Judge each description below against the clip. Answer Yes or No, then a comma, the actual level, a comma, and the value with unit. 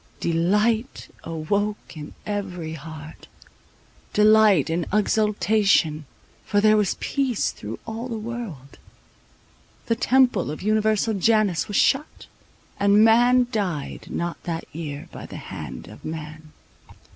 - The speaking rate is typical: No, slow, 120 wpm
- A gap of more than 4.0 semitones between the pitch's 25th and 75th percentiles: Yes, average, 5.2 semitones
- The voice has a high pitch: Yes, high, 205 Hz